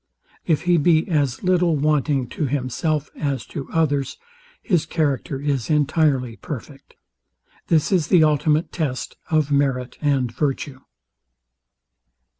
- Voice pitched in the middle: Yes, medium, 145 Hz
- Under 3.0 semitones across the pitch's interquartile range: Yes, narrow, 2.6 semitones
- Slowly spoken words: Yes, slow, 120 wpm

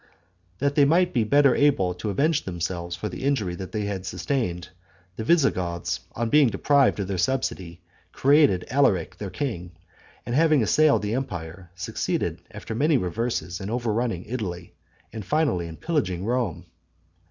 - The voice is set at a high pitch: No, low, 110 Hz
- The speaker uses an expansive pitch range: Yes, wide, 7.5 semitones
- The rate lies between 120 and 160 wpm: Yes, average, 155 wpm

